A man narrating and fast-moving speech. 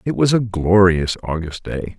No: male; average, 180 wpm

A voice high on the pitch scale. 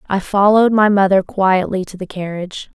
Yes: high, 195 Hz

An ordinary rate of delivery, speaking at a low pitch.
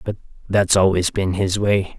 Yes: average, 180 wpm; very low, 95 Hz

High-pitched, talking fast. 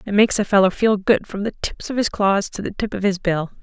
Yes: high, 200 Hz; fast, 300 wpm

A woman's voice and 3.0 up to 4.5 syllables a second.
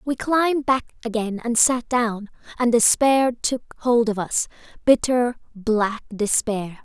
Yes: female; 3.9 syllables/s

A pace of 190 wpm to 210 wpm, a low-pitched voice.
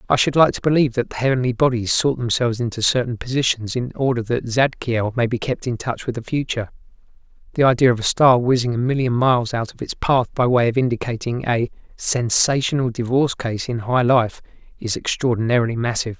Yes: average, 195 wpm; low, 120 Hz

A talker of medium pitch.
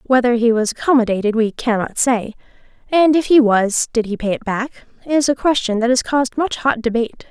No: high, 240 Hz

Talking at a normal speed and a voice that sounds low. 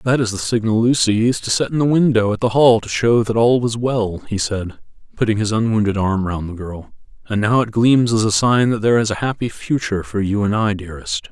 No: fast, 250 wpm; low, 110 Hz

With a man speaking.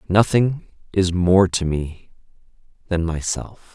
Yes: male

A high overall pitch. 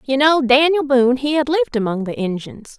Yes: very high, 270 Hz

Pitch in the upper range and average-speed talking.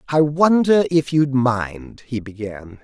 No: low, 135 Hz; average, 150 wpm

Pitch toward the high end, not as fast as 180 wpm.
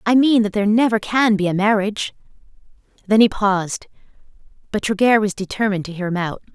No: high, 205 Hz; average, 185 wpm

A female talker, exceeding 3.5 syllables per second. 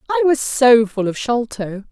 Yes: female; 4.3 syllables/s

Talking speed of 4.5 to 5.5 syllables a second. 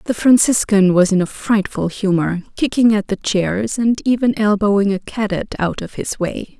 Yes: 4.7 syllables/s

